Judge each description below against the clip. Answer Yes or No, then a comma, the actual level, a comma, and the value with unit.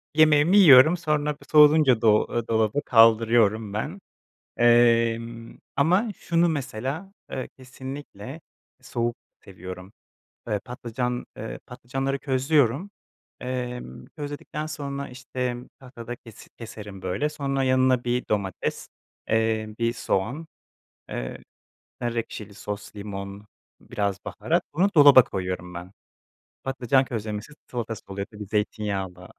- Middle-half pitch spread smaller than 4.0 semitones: No, average, 4.5 semitones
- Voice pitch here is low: Yes, low, 120 Hz